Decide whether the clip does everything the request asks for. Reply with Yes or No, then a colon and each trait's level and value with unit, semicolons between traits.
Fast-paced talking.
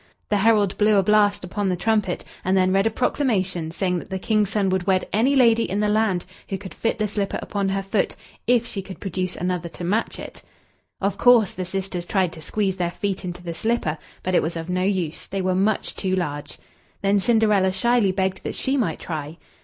Yes: fast, 220 wpm